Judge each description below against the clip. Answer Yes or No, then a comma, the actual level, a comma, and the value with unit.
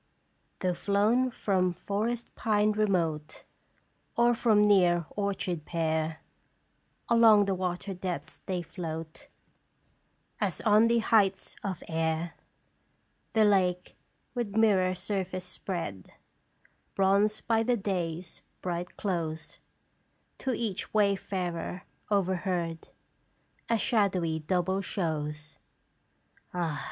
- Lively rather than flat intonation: No, average, 3.5 semitones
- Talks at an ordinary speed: No, slow, 105 wpm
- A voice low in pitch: No, high, 190 Hz